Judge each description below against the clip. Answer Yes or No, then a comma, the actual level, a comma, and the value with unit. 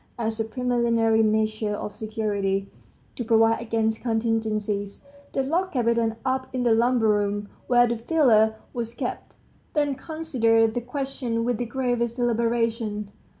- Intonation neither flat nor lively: No, narrow, 2.0 semitones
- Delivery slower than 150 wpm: Yes, average, 140 wpm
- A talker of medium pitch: No, high, 230 Hz